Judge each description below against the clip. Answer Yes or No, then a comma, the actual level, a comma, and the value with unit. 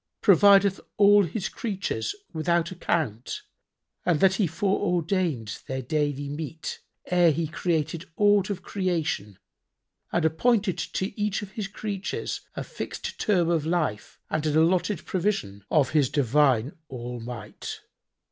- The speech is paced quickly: No, slow, 135 wpm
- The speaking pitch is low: No, medium, 170 Hz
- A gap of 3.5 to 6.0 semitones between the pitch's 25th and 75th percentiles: Yes, average, 5.0 semitones